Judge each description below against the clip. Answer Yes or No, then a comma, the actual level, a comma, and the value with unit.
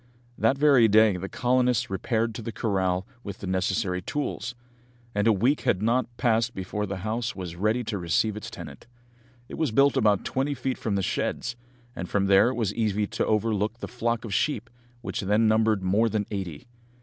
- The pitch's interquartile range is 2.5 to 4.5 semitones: Yes, average, 3.2 semitones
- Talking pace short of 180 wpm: No, average, 195 wpm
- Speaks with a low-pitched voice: Yes, low, 110 Hz